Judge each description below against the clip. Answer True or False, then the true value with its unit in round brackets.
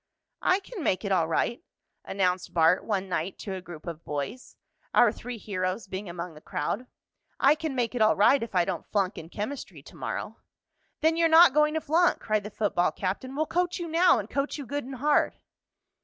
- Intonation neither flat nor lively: False (7.8 semitones)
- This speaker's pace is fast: True (210 wpm)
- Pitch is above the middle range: True (215 Hz)